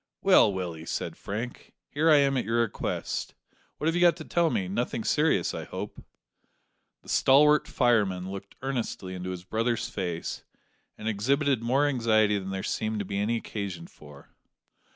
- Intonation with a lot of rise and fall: Yes, wide, 6.0 semitones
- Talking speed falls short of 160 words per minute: No, average, 170 wpm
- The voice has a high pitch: No, low, 110 Hz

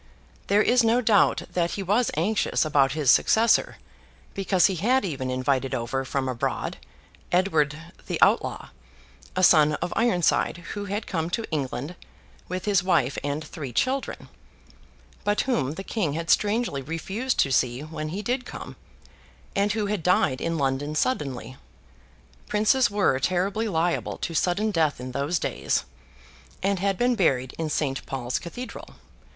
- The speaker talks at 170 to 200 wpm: No, average, 155 wpm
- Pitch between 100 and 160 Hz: No, medium, 175 Hz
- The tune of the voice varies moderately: No, wide, 6.6 semitones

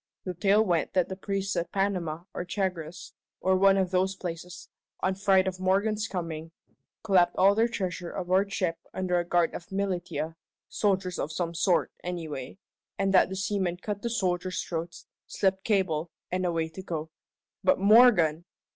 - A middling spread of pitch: No, narrow, 2.3 semitones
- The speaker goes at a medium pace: Yes, average, 165 wpm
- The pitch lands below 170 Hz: No, medium, 185 Hz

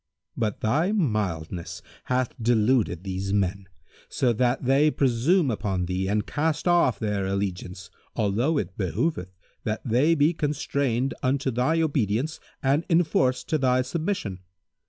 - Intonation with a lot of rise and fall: Yes, wide, 6.6 semitones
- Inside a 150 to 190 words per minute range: No, slow, 135 wpm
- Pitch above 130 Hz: No, low, 125 Hz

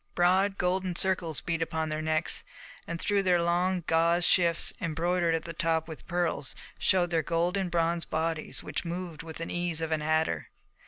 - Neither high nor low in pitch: Yes, medium, 170 Hz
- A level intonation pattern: Yes, narrow, 1.6 semitones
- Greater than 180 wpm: No, average, 175 wpm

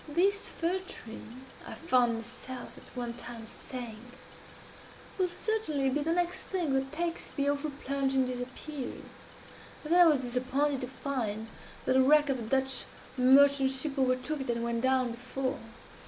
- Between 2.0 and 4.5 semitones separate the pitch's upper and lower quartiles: Yes, average, 2.9 semitones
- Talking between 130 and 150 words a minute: No, average, 165 wpm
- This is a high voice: Yes, very high, 265 Hz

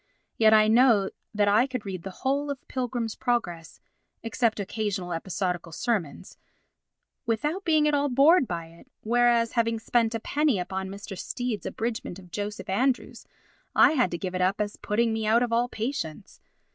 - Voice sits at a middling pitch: No, high, 225 Hz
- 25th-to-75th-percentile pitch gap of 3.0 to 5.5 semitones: Yes, average, 4.2 semitones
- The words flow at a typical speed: Yes, average, 175 wpm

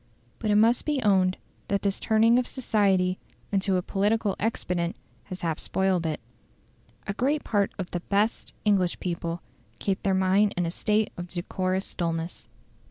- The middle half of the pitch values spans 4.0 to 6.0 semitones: No, average, 2.8 semitones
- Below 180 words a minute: Yes, average, 165 wpm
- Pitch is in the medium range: No, high, 195 Hz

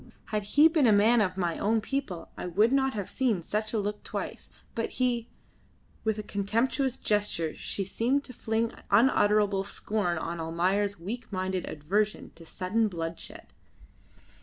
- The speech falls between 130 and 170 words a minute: Yes, average, 160 wpm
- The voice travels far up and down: No, average, 3.6 semitones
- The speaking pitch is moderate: No, high, 210 Hz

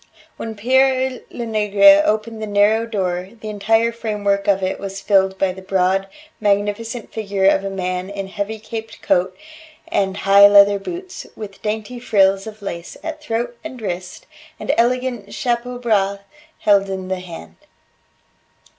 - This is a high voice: Yes, high, 205 Hz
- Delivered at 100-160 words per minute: Yes, average, 150 wpm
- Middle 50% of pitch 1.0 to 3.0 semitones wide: Yes, average, 2.7 semitones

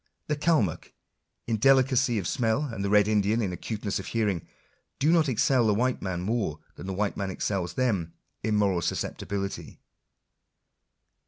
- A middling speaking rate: Yes, average, 160 wpm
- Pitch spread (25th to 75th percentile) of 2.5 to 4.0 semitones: No, average, 4.4 semitones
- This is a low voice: Yes, low, 105 Hz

